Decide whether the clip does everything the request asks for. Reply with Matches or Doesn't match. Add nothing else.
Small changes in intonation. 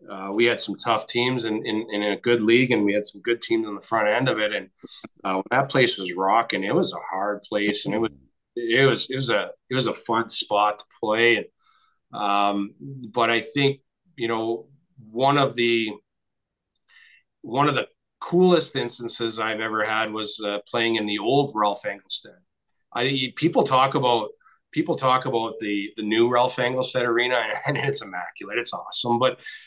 Doesn't match